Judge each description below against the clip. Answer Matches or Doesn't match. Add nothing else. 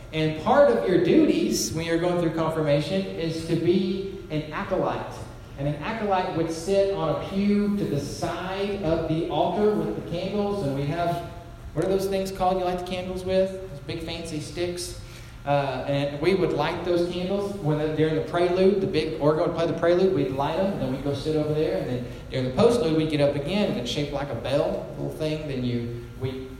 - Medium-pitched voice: Matches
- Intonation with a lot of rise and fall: Doesn't match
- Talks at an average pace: Doesn't match